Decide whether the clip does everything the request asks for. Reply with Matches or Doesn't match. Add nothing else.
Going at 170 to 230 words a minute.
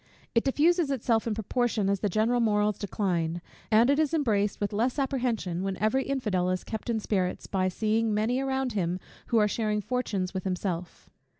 Matches